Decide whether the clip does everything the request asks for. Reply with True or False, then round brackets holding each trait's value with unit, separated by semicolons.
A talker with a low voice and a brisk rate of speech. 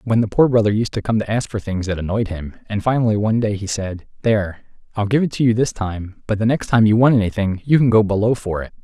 True (105 Hz; 280 wpm)